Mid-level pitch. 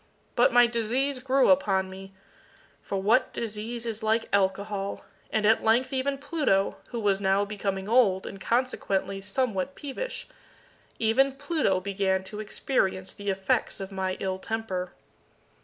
No: high, 215 Hz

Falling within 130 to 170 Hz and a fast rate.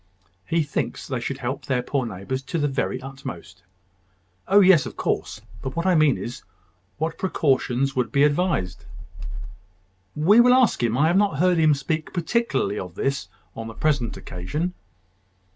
No: medium, 140 Hz; average, 165 wpm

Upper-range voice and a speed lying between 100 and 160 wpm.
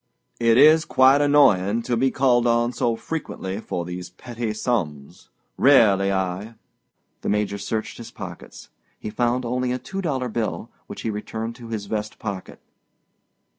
No: low, 115 Hz; average, 155 wpm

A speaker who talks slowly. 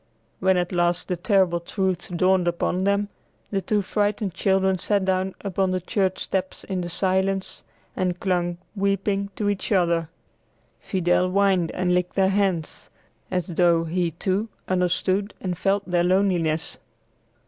No: average, 150 wpm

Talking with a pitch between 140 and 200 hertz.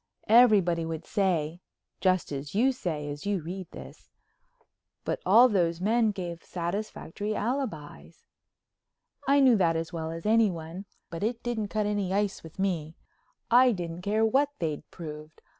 Yes: high, 190 Hz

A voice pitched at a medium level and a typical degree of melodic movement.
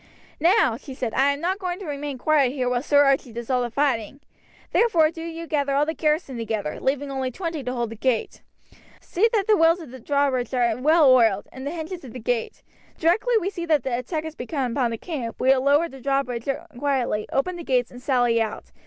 No: very high, 275 Hz; average, 4.5 semitones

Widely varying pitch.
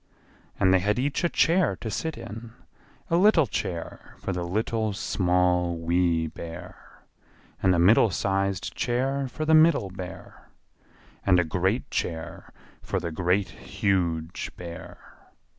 No: average, 5.0 semitones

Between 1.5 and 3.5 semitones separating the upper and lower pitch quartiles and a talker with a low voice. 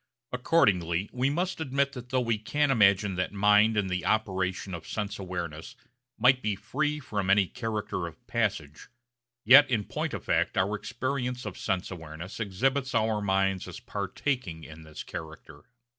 No: average, 5.2 semitones; low, 105 Hz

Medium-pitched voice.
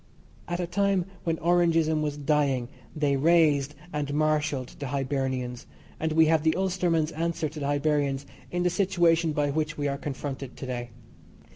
Yes: medium, 150 Hz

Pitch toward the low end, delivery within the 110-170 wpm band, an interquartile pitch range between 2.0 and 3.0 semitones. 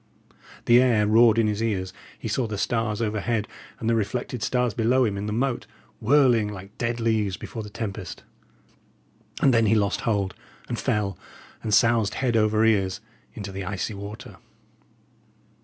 Yes: low, 110 Hz; average, 165 wpm; narrow, 2.4 semitones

